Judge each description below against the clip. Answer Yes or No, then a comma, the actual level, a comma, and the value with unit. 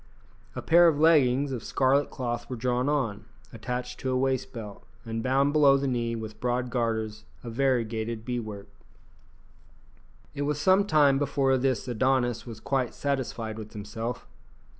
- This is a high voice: No, low, 125 Hz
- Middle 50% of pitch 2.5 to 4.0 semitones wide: Yes, average, 3.2 semitones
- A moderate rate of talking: Yes, average, 160 wpm